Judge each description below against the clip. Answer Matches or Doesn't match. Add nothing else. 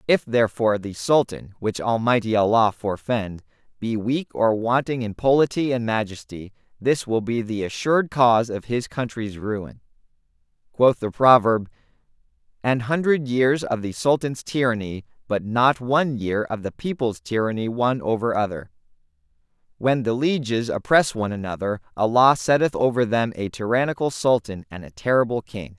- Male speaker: Matches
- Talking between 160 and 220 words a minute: Doesn't match